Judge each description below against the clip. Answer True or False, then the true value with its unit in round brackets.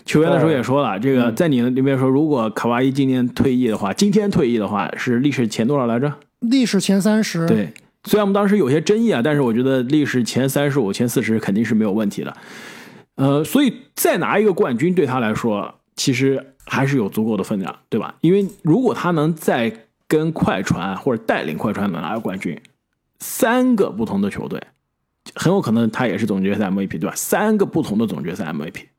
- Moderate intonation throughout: False (8.4 semitones)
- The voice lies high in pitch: False (145 Hz)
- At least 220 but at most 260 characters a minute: False (325 characters per minute)